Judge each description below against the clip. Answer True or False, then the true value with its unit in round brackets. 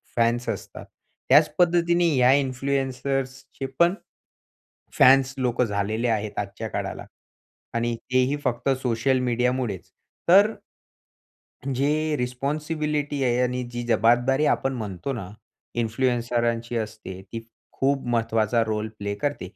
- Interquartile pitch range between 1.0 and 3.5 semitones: True (2.9 semitones)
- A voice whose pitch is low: True (125 Hz)